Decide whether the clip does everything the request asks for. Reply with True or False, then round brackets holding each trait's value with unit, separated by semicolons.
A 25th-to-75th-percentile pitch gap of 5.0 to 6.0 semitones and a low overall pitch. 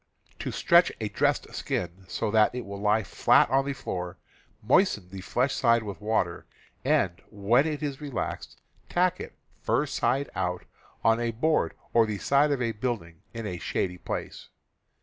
True (5.6 semitones; 110 Hz)